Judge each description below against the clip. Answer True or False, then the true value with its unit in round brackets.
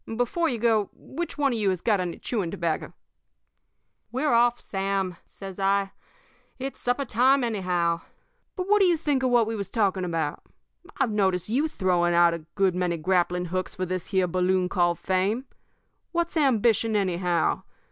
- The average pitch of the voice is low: False (195 Hz)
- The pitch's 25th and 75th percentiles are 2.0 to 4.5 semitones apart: False (5.1 semitones)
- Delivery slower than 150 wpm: False (170 wpm)